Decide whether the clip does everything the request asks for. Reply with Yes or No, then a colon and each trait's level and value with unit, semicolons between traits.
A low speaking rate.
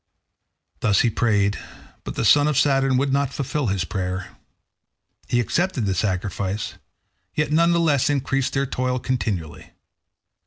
No: average, 145 wpm